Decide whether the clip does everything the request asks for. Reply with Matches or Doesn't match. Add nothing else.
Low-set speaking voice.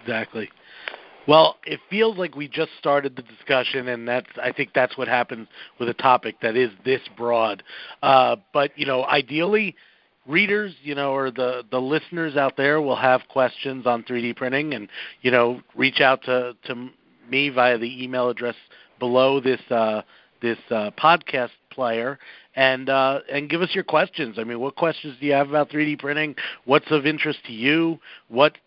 Matches